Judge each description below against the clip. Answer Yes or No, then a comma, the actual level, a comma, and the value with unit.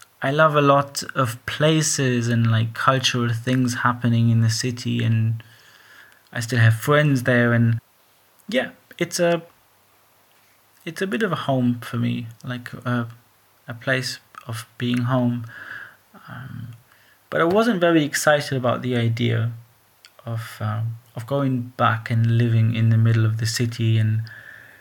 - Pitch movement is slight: Yes, narrow, 2.3 semitones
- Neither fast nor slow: Yes, average, 150 wpm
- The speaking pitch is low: Yes, low, 120 Hz